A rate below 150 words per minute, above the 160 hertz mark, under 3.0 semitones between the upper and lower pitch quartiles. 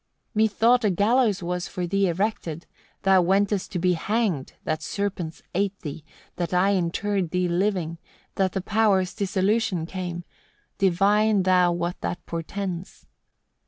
Yes: average, 140 wpm; medium, 185 Hz; narrow, 2.6 semitones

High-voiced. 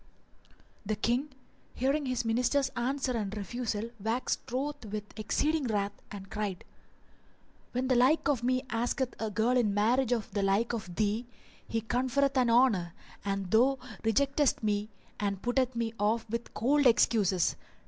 Yes: high, 235 Hz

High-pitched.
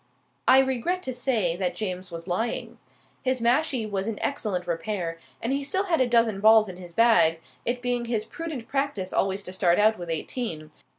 Yes: high, 220 Hz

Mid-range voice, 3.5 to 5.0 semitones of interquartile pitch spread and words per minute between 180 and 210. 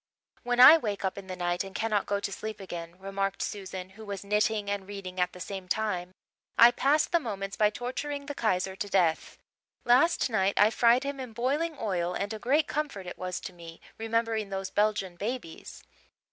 No: high, 205 Hz; average, 3.8 semitones; average, 200 wpm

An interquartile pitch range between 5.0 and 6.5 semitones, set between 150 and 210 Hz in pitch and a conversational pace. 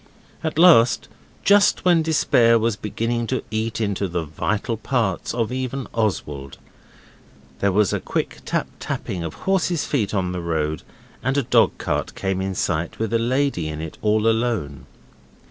No: wide, 5.6 semitones; low, 110 Hz; average, 160 wpm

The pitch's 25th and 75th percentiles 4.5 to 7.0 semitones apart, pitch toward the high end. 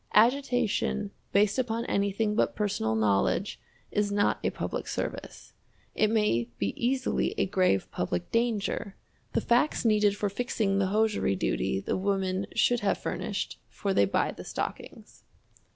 No: average, 2.9 semitones; high, 205 Hz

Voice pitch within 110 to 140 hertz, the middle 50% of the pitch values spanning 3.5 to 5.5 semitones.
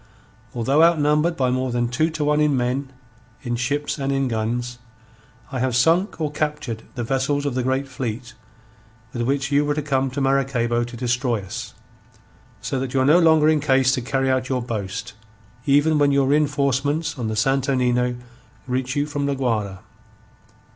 No: low, 135 Hz; average, 2.8 semitones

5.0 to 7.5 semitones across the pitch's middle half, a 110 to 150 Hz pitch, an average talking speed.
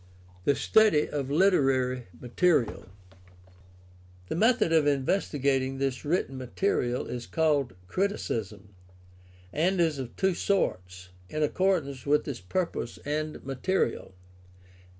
No: wide, 5.4 semitones; medium, 140 Hz; slow, 110 wpm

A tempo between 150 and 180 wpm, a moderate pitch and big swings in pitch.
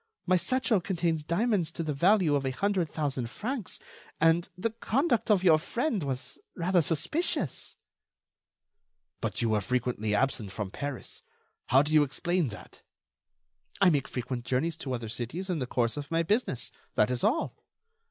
Yes: average, 160 wpm; medium, 155 Hz; wide, 6.6 semitones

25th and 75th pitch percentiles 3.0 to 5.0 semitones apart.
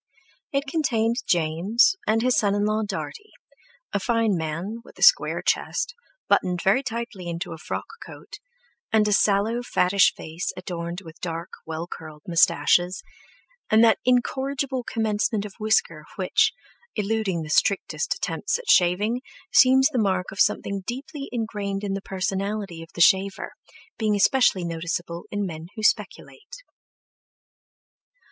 Yes: average, 4.7 semitones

